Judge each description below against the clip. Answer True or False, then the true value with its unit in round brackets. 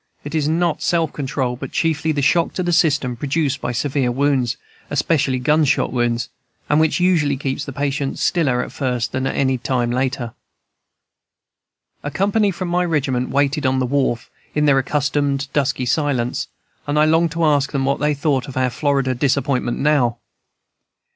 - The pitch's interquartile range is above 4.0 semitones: False (2.7 semitones)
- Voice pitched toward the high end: False (140 Hz)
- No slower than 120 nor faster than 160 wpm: False (170 wpm)